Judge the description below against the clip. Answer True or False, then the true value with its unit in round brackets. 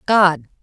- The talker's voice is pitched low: False (195 Hz)